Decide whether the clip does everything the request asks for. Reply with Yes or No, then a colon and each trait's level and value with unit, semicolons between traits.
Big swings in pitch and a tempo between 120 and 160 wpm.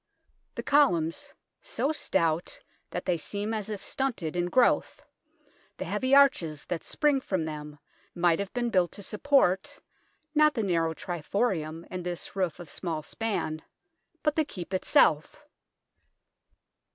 Yes: wide, 6.3 semitones; average, 140 wpm